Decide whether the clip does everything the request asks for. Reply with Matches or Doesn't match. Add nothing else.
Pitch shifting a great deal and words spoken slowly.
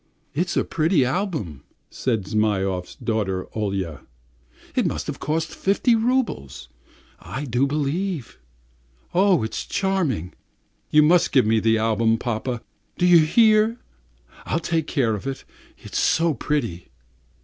Matches